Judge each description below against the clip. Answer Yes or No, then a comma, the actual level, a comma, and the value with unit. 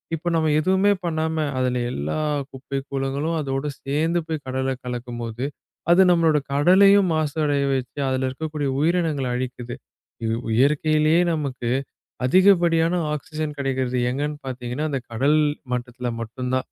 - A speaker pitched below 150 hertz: Yes, medium, 140 Hz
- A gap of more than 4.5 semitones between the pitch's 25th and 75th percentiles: No, average, 3.7 semitones